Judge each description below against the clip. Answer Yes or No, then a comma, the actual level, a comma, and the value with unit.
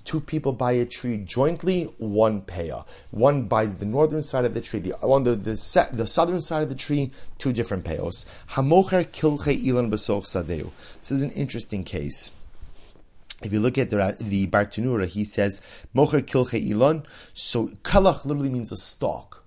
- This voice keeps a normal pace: Yes, average, 165 wpm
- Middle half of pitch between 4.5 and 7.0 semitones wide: Yes, wide, 5.5 semitones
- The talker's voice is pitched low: Yes, low, 120 Hz